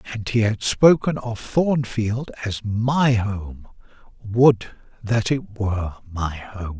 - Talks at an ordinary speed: No, slow, 125 wpm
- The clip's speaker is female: No, male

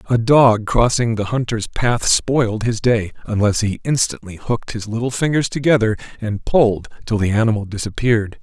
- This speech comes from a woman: No, male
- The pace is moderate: Yes, average, 165 wpm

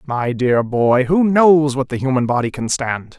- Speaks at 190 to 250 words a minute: Yes, fast, 205 wpm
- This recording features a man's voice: Yes, male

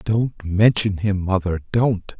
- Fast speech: No, slow, 135 wpm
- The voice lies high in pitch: No, low, 100 Hz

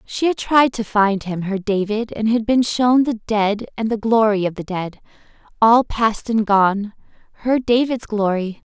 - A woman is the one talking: Yes, female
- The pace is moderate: Yes, average, 170 wpm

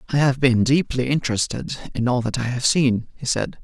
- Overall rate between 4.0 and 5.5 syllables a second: Yes, 5.3 syllables/s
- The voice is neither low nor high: No, low, 125 Hz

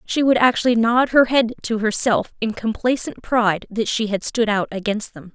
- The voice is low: No, high, 225 Hz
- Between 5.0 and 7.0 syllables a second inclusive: Yes, 5.1 syllables/s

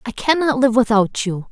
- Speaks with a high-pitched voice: Yes, high, 240 Hz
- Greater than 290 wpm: No, average, 200 wpm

